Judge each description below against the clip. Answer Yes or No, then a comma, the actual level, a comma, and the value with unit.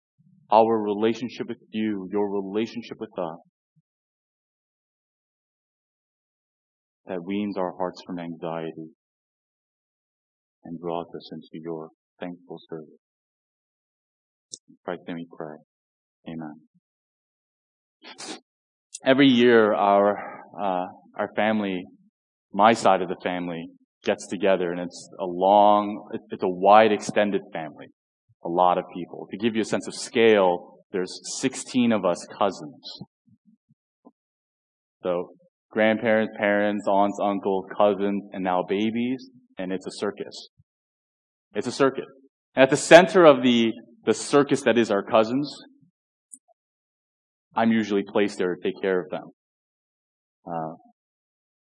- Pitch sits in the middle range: No, low, 100 Hz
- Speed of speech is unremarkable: No, slow, 115 wpm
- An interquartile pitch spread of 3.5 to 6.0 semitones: Yes, average, 4.5 semitones